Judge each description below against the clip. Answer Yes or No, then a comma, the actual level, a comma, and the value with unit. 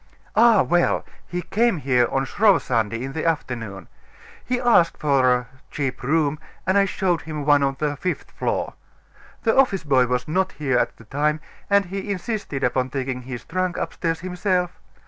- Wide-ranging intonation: Yes, wide, 6.0 semitones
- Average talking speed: Yes, average, 175 wpm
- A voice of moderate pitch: Yes, medium, 155 Hz